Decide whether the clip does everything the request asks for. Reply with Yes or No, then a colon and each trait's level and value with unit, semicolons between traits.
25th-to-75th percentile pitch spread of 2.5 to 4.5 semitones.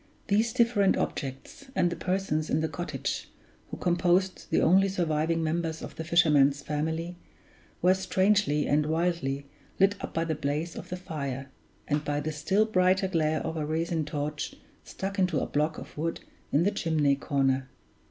Yes: average, 3.6 semitones